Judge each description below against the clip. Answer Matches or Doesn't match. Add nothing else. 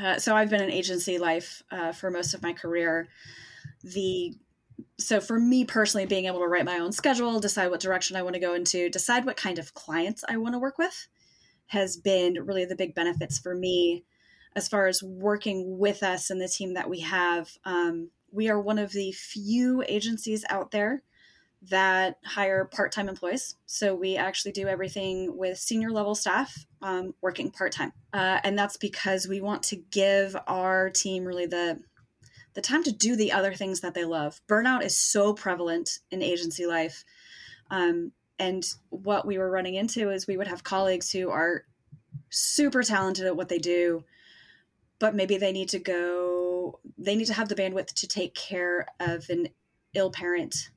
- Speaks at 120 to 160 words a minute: Doesn't match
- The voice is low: Doesn't match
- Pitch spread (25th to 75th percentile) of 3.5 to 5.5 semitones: Doesn't match